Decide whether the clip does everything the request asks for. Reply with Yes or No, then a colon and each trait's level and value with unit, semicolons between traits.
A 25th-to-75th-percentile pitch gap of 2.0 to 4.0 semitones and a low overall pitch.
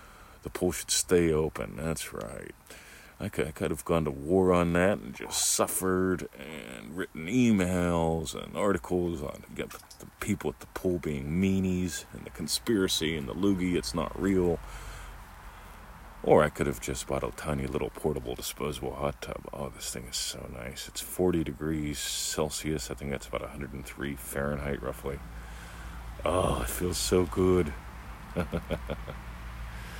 No: average, 4.4 semitones; very low, 80 Hz